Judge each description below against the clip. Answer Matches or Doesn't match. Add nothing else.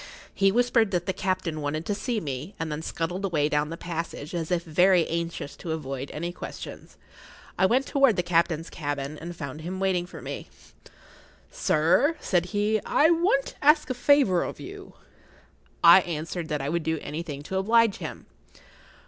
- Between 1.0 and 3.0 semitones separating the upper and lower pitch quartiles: Doesn't match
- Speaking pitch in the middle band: Matches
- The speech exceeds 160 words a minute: Matches